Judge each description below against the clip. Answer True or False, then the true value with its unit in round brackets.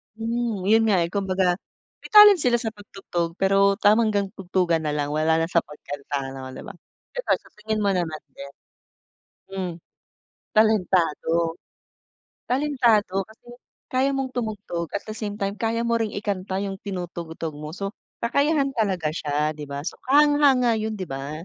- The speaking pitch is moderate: False (195 Hz)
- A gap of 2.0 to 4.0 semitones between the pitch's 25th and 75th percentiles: False (4.9 semitones)